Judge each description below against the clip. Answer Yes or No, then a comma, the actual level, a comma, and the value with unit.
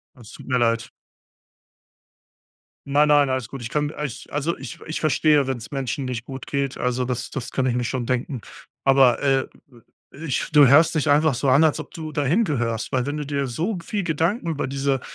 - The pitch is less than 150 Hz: Yes, medium, 140 Hz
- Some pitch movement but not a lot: Yes, average, 3.0 semitones